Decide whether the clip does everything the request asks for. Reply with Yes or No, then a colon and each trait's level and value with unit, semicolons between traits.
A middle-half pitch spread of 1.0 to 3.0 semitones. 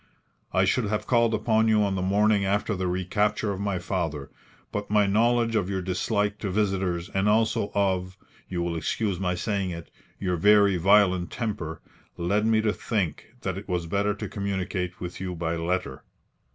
Yes: narrow, 2.6 semitones